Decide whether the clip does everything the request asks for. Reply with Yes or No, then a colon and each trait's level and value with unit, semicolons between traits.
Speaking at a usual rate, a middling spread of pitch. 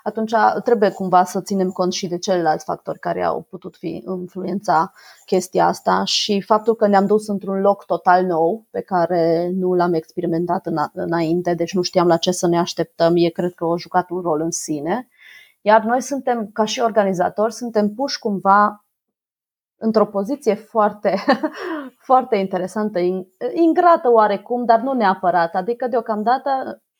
Yes: average, 160 wpm; average, 4.1 semitones